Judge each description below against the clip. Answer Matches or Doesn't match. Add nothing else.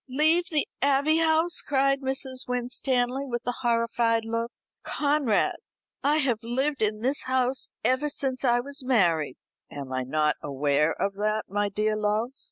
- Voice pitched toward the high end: Matches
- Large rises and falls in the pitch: Doesn't match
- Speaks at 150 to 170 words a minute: Matches